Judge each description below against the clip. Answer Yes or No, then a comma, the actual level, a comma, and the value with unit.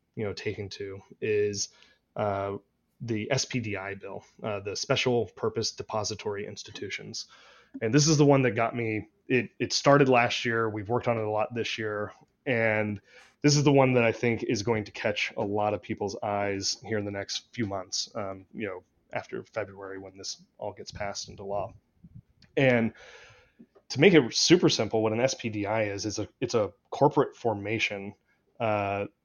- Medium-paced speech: Yes, average, 180 wpm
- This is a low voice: Yes, low, 110 Hz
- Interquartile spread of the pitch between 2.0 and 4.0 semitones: Yes, average, 3.1 semitones